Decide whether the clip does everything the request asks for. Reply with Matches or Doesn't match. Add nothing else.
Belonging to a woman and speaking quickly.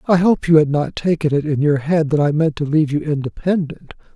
Doesn't match